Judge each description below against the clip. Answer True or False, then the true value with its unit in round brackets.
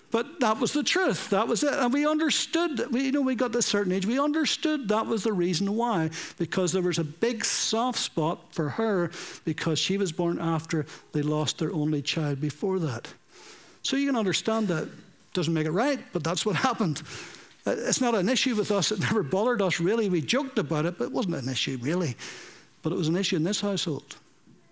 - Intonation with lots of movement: True (6.7 semitones)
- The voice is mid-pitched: False (200 Hz)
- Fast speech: True (220 wpm)